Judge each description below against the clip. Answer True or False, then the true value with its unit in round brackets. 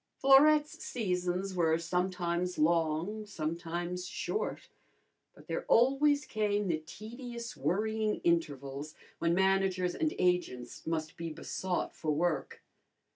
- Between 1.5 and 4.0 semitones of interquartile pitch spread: False (4.5 semitones)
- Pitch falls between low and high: True (180 Hz)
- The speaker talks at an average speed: False (110 wpm)